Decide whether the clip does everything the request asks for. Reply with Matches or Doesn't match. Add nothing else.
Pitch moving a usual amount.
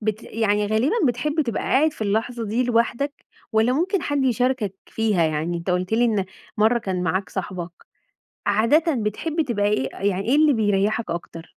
Matches